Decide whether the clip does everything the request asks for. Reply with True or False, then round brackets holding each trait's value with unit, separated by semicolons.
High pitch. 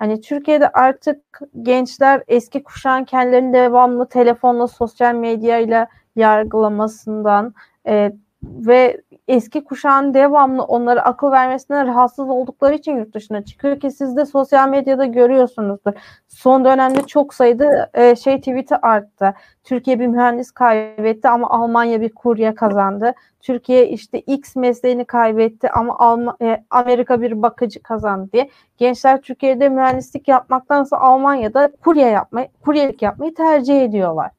True (250 Hz)